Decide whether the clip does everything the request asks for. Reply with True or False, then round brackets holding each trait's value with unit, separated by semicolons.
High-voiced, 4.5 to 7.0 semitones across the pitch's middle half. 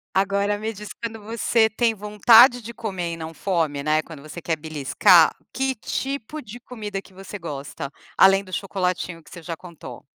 True (195 Hz; 4.9 semitones)